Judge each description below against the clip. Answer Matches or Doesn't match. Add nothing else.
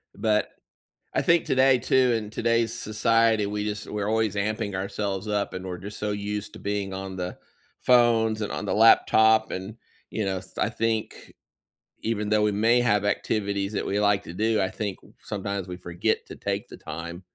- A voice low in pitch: Matches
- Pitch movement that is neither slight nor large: Doesn't match